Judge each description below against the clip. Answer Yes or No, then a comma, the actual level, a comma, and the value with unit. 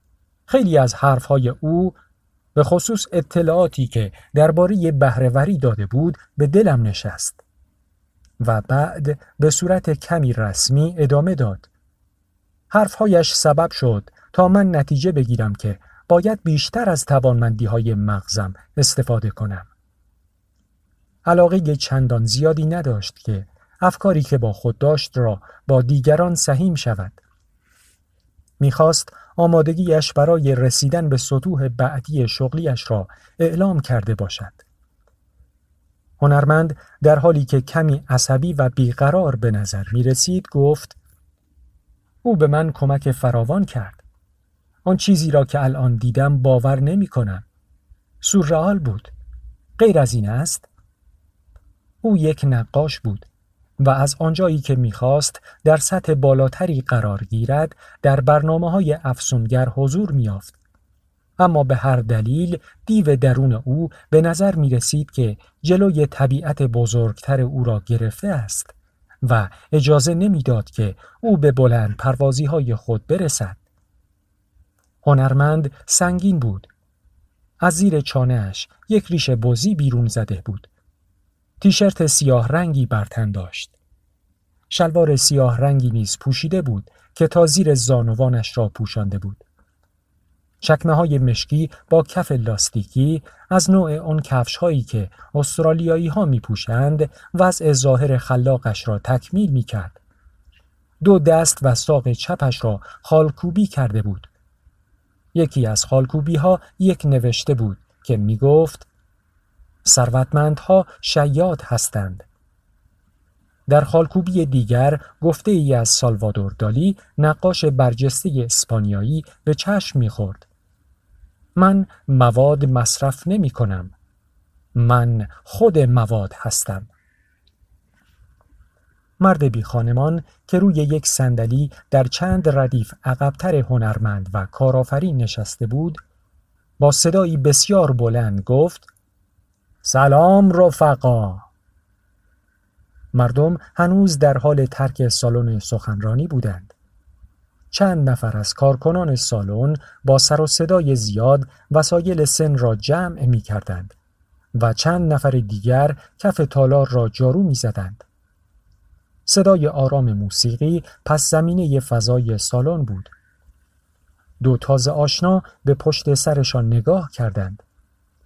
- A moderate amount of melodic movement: No, wide, 7.1 semitones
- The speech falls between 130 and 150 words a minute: No, average, 115 wpm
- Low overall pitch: Yes, low, 130 Hz